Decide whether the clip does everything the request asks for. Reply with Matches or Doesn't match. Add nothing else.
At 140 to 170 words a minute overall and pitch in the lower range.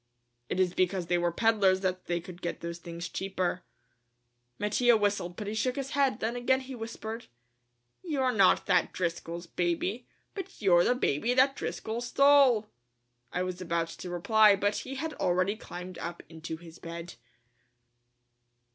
Doesn't match